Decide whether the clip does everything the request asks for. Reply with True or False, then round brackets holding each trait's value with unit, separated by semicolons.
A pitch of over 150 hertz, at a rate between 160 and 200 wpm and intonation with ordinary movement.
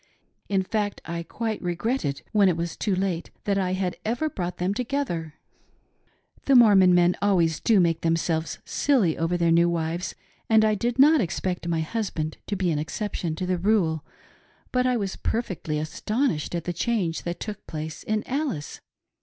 True (185 Hz; 180 wpm; 4.5 semitones)